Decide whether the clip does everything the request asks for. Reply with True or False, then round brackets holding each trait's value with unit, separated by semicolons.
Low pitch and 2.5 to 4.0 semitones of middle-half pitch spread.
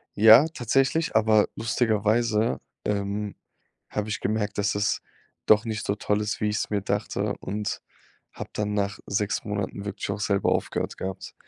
False (105 Hz; 1.2 semitones)